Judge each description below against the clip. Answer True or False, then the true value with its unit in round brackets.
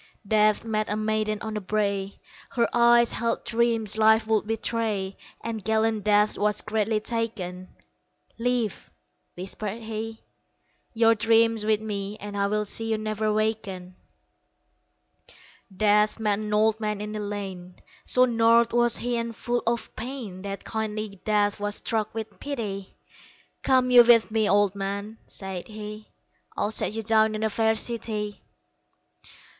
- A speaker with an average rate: True (150 wpm)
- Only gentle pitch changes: True (1.5 semitones)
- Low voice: False (215 Hz)